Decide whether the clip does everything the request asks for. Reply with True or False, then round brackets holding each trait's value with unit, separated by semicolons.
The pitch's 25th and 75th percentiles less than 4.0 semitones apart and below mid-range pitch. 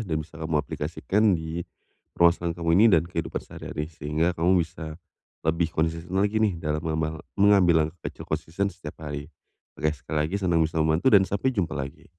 True (2.8 semitones; 80 Hz)